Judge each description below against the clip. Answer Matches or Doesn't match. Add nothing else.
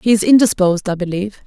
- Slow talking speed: Doesn't match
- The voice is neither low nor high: Doesn't match